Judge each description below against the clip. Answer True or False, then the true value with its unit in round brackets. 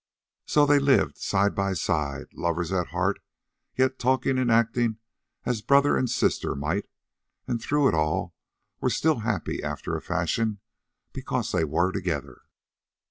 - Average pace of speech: True (145 wpm)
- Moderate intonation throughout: False (6.9 semitones)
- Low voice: True (105 Hz)